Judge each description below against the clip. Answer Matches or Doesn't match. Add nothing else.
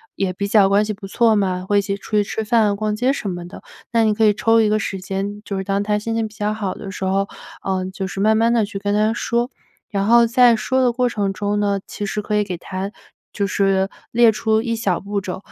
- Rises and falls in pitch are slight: Matches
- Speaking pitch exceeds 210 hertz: Doesn't match